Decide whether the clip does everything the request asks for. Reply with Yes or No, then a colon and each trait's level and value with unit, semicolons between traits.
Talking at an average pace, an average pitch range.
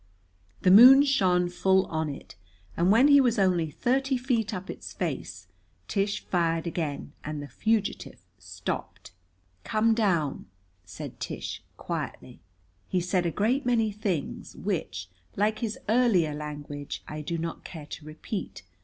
No: average, 145 wpm; wide, 5.9 semitones